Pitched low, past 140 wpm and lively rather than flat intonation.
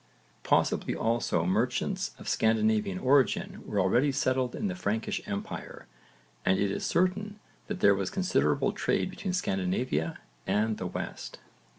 No: low, 110 Hz; slow, 135 wpm; wide, 7.0 semitones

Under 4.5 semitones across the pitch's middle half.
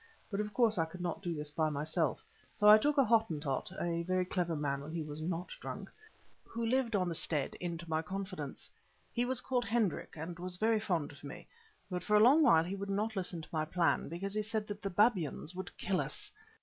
No: average, 4.8 semitones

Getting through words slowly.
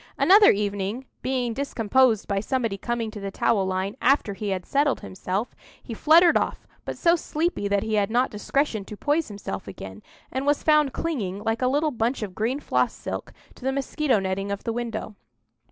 No: average, 190 wpm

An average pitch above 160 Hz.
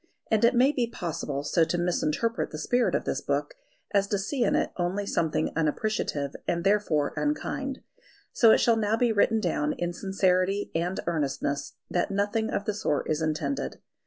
Yes: high, 190 Hz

